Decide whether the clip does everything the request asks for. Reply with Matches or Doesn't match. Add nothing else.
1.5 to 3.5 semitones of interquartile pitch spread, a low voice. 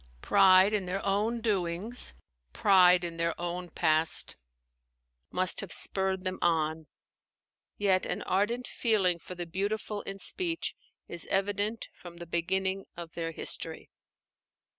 Doesn't match